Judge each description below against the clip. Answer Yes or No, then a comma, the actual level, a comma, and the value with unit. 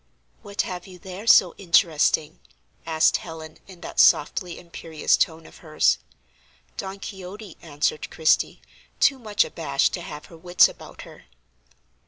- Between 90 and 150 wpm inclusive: Yes, average, 140 wpm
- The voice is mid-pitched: Yes, medium, 170 Hz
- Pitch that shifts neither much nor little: Yes, average, 3.2 semitones